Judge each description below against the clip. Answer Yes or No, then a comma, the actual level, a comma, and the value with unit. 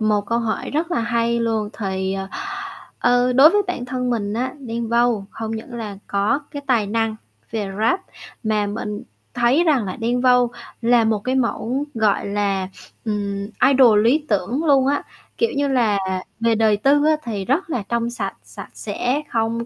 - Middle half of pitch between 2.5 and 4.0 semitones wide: Yes, average, 3.2 semitones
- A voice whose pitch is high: Yes, high, 230 Hz